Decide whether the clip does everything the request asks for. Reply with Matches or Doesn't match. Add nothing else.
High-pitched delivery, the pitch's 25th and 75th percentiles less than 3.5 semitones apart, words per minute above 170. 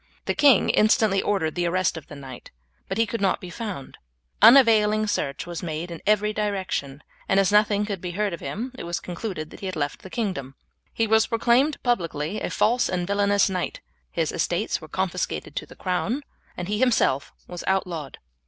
Doesn't match